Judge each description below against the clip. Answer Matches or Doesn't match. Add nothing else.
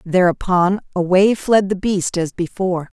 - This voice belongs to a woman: Matches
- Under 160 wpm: Matches